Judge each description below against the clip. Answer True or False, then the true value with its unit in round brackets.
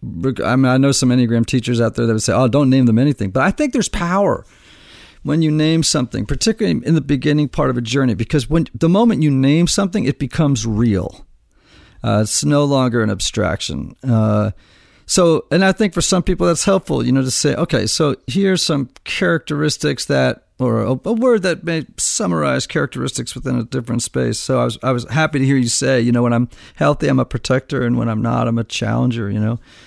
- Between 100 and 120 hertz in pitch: False (135 Hz)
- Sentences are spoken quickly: True (220 wpm)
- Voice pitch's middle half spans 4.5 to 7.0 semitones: True (5.0 semitones)